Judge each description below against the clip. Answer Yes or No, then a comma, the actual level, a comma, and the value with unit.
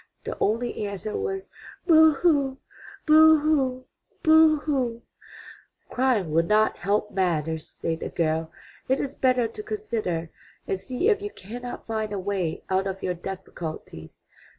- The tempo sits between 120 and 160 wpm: Yes, average, 145 wpm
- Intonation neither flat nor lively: No, wide, 7.9 semitones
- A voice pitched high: Yes, high, 225 Hz